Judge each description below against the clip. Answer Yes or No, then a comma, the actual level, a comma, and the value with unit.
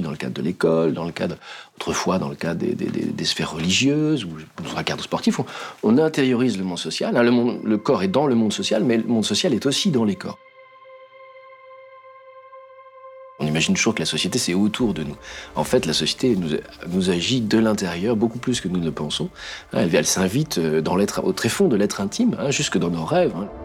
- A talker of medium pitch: No, low, 120 Hz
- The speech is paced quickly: Yes, fast, 225 wpm